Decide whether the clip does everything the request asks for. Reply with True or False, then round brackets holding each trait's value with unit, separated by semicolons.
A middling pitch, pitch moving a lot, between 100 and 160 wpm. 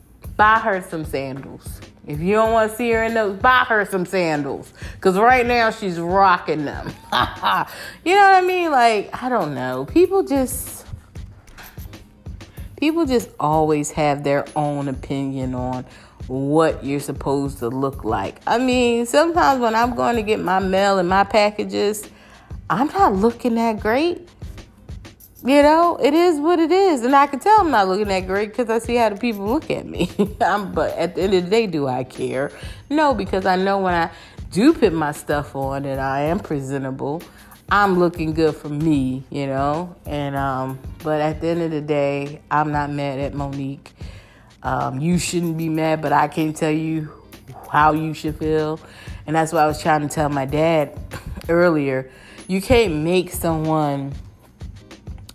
False (160 Hz; 8.0 semitones; 180 wpm)